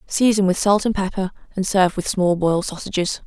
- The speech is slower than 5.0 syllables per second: No, 5.9 syllables/s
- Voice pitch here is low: No, high, 190 Hz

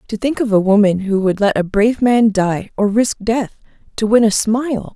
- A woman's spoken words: Yes, female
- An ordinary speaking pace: No, fast, 230 wpm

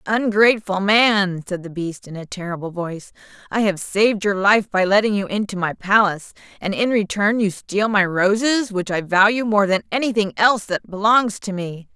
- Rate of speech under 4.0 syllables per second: No, 5.1 syllables/s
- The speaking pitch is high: Yes, high, 200 Hz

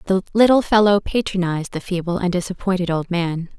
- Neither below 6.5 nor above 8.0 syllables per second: No, 5.9 syllables/s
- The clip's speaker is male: No, female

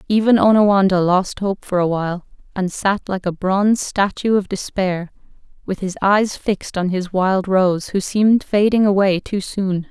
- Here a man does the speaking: No, female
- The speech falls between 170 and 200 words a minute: Yes, average, 175 wpm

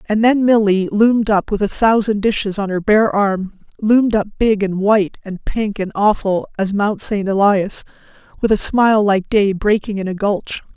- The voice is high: Yes, high, 205 Hz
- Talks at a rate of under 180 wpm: No, average, 185 wpm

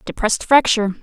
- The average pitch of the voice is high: Yes, high, 230 Hz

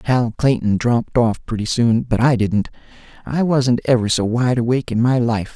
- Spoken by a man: Yes, male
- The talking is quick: No, average, 195 wpm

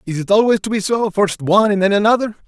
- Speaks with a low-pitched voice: No, high, 205 Hz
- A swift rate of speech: Yes, fast, 245 wpm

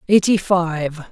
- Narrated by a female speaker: No, male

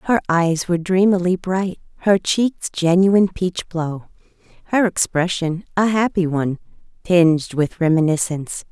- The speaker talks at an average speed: No, slow, 115 wpm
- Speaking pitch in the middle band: Yes, medium, 175 Hz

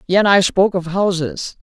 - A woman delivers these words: Yes, female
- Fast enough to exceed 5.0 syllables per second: No, 4.9 syllables/s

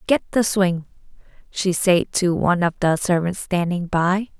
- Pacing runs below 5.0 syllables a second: Yes, 4.3 syllables/s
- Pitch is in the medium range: Yes, medium, 180 Hz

